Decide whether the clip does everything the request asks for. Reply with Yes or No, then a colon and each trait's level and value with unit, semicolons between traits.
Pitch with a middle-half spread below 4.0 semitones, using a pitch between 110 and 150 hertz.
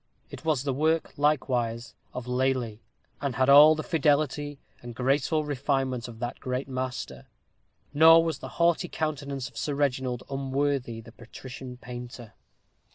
Yes: average, 2.9 semitones; low, 135 Hz